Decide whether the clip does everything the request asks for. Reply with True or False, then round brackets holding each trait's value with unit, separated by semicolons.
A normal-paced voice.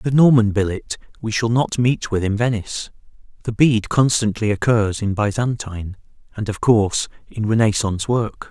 True (155 wpm)